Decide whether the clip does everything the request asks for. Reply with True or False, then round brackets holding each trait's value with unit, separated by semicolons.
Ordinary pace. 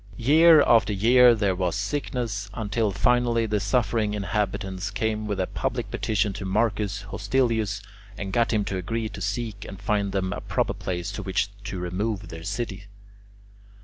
True (165 wpm)